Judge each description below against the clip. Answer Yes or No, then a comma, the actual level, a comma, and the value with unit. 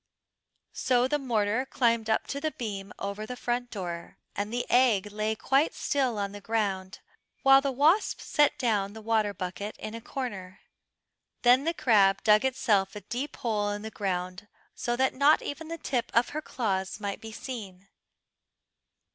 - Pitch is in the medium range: No, high, 220 Hz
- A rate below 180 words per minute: Yes, average, 170 wpm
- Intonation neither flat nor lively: Yes, average, 4.3 semitones